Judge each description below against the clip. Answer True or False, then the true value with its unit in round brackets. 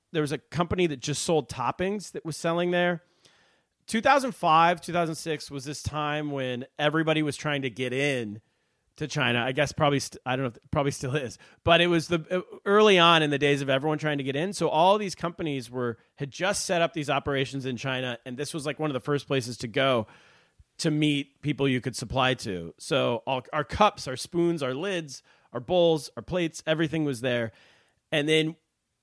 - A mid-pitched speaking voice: True (150 Hz)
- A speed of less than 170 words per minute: False (205 wpm)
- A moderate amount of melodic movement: True (4.0 semitones)